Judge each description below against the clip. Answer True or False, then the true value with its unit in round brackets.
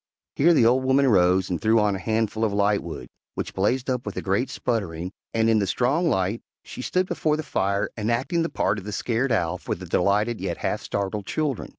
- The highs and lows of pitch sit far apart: False (4.7 semitones)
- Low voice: True (110 Hz)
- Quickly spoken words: True (220 wpm)